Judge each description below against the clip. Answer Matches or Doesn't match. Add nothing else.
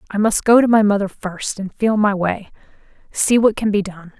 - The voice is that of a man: Doesn't match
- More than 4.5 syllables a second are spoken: Matches